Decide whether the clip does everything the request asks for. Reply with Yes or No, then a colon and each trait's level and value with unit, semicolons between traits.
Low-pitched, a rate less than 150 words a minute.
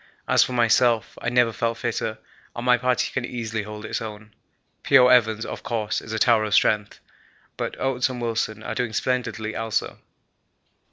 No: low, 115 Hz; average, 175 wpm